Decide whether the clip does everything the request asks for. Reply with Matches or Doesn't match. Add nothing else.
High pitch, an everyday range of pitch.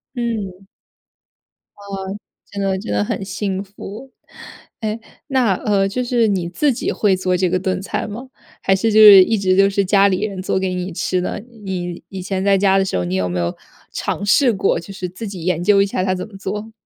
Doesn't match